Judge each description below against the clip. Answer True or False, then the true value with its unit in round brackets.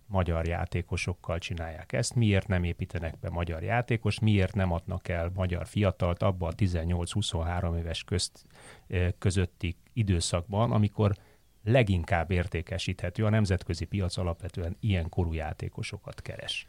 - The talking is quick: False (120 wpm)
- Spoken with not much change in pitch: False (3.3 semitones)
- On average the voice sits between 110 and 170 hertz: False (95 Hz)